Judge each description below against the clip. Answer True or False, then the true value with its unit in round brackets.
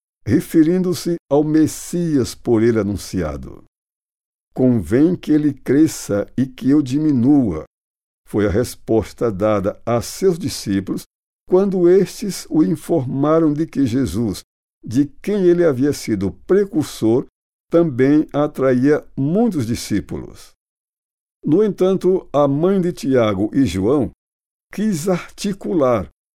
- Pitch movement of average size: False (6.8 semitones)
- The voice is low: False (145 Hz)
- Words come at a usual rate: False (110 wpm)